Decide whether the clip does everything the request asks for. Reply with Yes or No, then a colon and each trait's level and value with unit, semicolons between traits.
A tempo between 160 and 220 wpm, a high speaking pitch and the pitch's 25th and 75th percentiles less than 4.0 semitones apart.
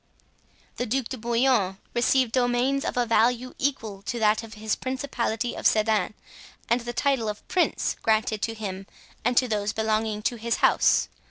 Yes: average, 170 wpm; high, 230 Hz; narrow, 2.5 semitones